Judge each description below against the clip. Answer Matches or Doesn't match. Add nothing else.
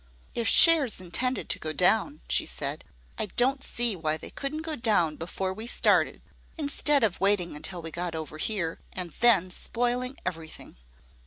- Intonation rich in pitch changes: Matches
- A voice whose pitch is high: Matches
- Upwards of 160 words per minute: Matches